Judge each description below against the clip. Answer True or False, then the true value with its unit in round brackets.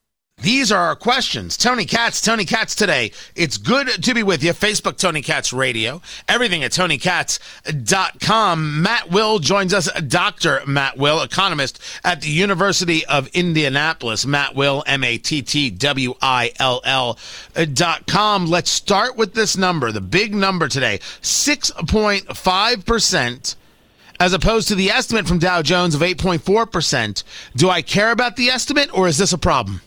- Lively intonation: True (6.1 semitones)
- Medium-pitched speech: True (175 Hz)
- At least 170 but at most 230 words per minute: False (145 wpm)